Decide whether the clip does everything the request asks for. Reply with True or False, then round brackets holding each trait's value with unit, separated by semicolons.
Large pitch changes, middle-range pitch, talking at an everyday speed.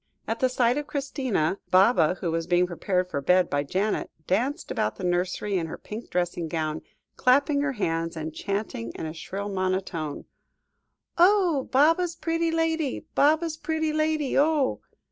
False (9.0 semitones; 205 Hz; 155 wpm)